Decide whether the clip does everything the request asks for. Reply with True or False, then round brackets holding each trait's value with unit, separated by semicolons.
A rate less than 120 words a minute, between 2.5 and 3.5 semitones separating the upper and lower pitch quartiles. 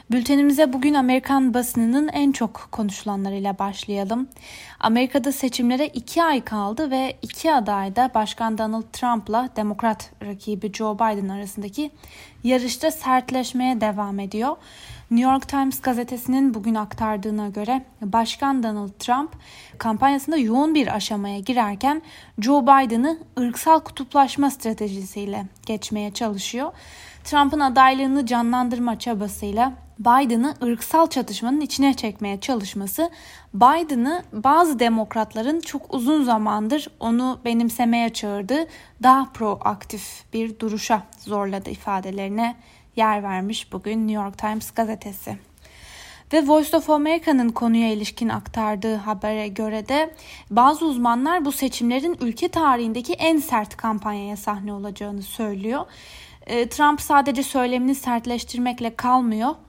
False (110 wpm; 4.2 semitones)